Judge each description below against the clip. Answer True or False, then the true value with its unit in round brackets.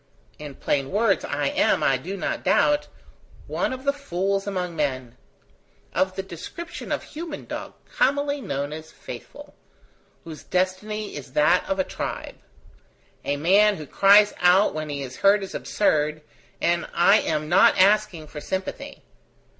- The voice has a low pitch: False (185 Hz)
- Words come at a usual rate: True (155 wpm)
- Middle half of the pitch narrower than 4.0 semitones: False (5.4 semitones)